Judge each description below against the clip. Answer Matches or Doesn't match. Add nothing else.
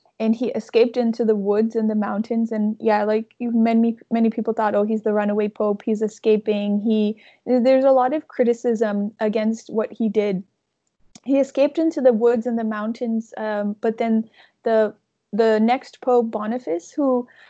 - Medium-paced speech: Matches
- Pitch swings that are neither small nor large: Doesn't match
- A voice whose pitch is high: Matches